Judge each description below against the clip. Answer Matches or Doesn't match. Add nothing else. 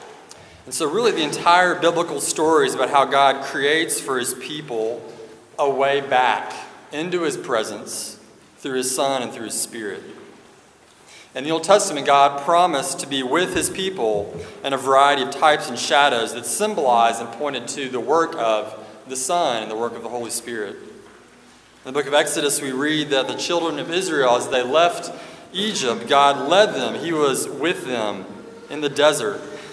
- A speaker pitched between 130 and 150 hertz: Matches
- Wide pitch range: Doesn't match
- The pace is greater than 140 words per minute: Matches